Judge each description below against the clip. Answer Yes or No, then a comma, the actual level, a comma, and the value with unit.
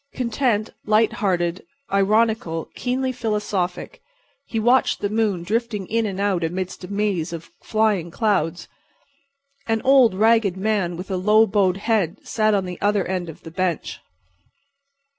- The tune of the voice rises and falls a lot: No, average, 3.4 semitones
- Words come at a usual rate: Yes, average, 145 wpm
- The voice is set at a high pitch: Yes, high, 205 Hz